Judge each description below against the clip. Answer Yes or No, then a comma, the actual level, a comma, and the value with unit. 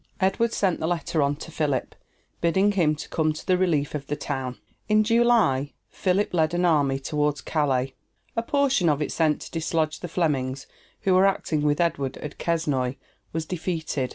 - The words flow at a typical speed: Yes, average, 180 wpm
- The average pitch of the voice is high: No, medium, 160 Hz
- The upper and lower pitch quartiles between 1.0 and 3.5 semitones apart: No, average, 4.0 semitones